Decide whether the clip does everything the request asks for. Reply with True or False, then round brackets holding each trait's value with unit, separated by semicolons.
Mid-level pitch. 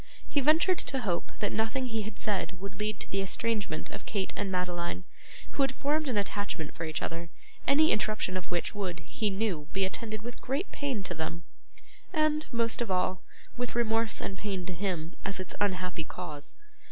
False (205 Hz)